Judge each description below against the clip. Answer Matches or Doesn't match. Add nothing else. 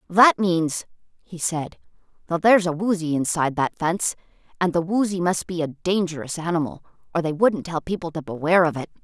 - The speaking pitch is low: Doesn't match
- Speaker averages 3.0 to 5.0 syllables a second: Doesn't match